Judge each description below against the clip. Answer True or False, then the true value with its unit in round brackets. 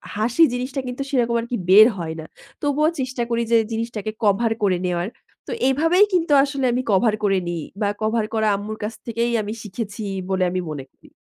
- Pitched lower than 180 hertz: False (225 Hz)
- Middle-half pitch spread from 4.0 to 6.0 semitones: False (3.6 semitones)